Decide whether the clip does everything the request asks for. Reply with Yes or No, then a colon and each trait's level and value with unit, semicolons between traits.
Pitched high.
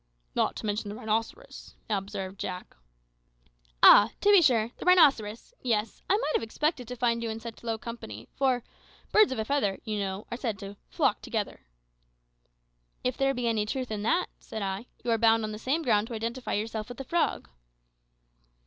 Yes: high, 225 Hz